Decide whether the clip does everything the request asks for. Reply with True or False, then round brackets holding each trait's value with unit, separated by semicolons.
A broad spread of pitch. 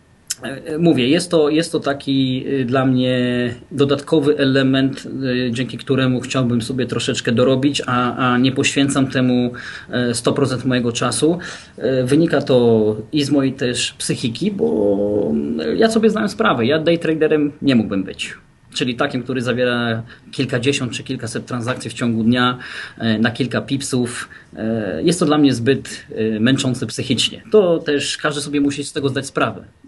False (2.7 semitones)